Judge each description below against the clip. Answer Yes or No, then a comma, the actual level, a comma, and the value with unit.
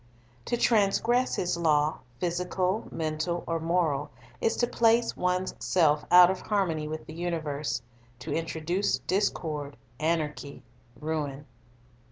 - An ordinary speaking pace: No, slow, 120 wpm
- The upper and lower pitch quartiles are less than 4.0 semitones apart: Yes, average, 3.3 semitones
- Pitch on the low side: No, medium, 165 Hz